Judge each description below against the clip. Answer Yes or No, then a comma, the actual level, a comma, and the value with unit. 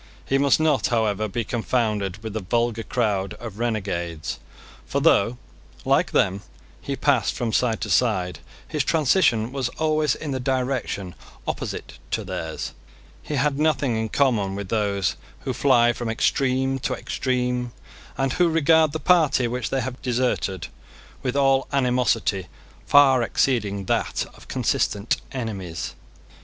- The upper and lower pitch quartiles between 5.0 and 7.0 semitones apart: No, average, 4.2 semitones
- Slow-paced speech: No, average, 145 wpm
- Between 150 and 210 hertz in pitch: No, low, 120 Hz